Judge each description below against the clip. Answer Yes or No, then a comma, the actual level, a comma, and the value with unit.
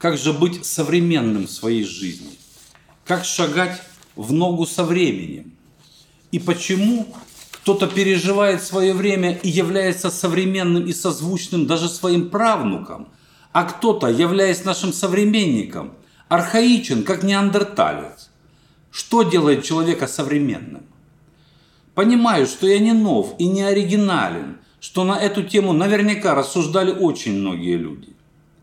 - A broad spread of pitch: No, average, 3.6 semitones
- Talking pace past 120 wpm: No, average, 115 wpm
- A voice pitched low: No, medium, 180 Hz